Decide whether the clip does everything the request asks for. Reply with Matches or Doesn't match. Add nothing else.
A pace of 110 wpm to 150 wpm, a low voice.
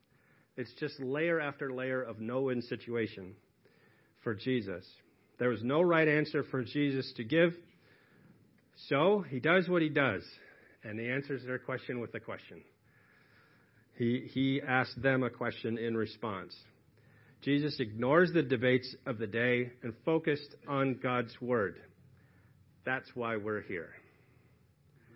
Matches